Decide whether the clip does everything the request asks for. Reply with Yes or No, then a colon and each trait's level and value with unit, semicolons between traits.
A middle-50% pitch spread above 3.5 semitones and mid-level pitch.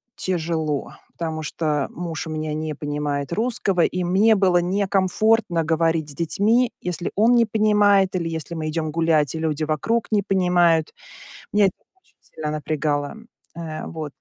Yes: average, 3.9 semitones; medium, 165 Hz